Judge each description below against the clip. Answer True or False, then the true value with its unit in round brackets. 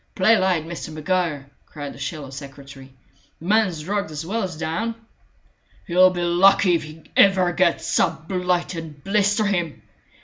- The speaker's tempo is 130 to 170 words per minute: True (160 wpm)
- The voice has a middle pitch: True (175 Hz)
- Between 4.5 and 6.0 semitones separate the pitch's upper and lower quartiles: False (3.5 semitones)